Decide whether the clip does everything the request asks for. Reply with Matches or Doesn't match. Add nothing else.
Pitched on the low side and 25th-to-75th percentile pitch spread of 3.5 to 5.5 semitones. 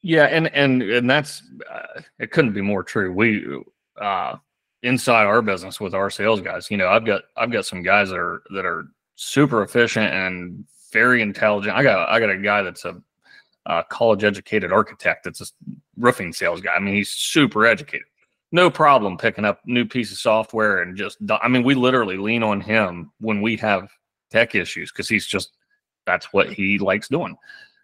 Matches